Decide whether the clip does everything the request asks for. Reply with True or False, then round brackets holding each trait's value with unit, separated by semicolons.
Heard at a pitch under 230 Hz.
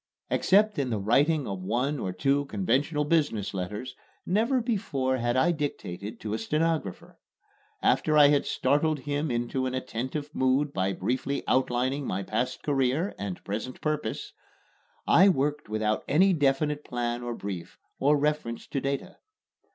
True (135 Hz)